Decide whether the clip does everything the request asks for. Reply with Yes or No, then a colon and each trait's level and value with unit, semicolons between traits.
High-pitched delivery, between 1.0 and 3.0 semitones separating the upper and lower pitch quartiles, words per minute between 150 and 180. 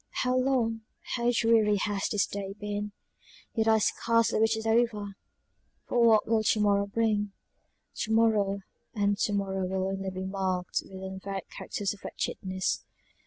Yes: high, 205 Hz; narrow, 2.5 semitones; average, 155 wpm